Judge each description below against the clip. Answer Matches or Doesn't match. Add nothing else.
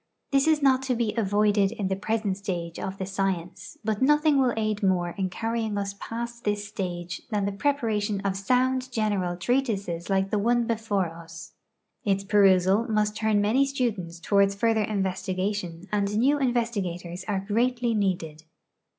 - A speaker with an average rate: Matches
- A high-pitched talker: Matches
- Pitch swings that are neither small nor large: Matches